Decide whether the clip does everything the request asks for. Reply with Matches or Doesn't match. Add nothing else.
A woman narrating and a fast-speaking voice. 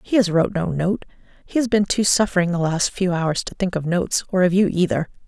Matches